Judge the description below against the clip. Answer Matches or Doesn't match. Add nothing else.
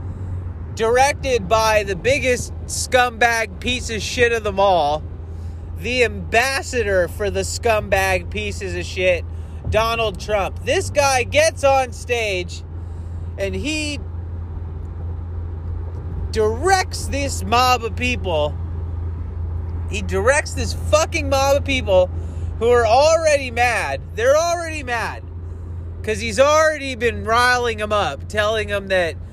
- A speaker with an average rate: Doesn't match